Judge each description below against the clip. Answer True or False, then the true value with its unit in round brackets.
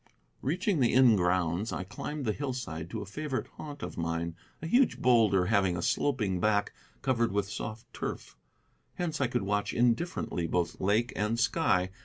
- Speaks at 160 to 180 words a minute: True (170 wpm)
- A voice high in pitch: False (110 Hz)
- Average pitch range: False (5.9 semitones)